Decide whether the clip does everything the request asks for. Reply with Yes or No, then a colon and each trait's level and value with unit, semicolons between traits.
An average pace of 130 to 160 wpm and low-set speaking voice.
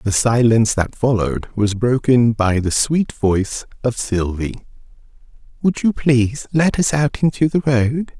Yes: average, 155 wpm; low, 120 Hz